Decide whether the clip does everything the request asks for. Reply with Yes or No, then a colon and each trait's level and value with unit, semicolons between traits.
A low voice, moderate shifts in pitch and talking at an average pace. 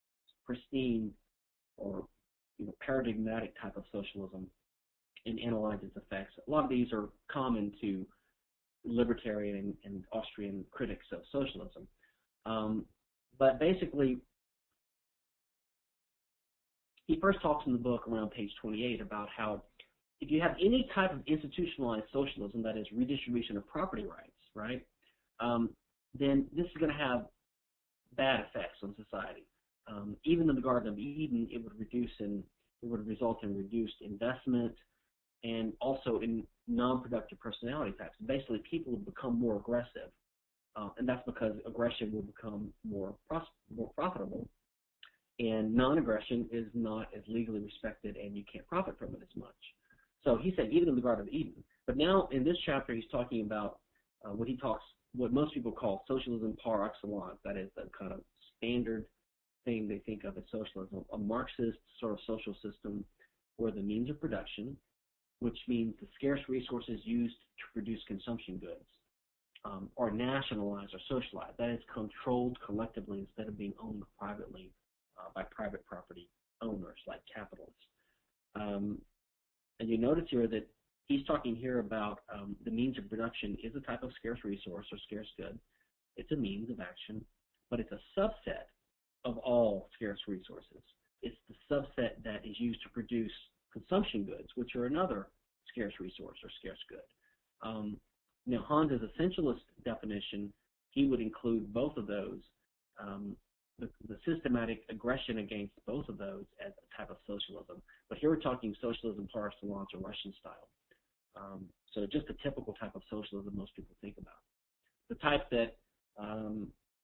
Yes: low, 115 Hz; average, 3.4 semitones; average, 155 wpm